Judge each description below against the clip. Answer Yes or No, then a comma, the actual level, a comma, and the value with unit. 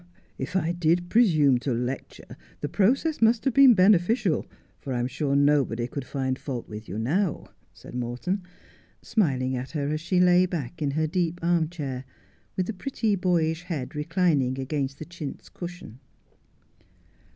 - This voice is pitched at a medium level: Yes, medium, 155 Hz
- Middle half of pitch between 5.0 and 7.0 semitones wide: Yes, average, 5.3 semitones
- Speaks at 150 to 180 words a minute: Yes, average, 160 wpm